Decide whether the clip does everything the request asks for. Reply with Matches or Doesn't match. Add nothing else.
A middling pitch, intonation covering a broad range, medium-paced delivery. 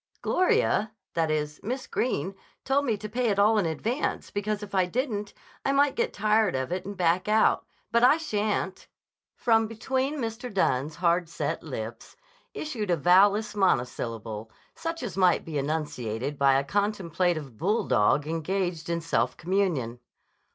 Doesn't match